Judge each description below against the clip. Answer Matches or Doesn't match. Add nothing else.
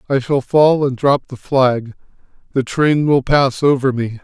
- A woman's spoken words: Doesn't match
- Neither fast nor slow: Matches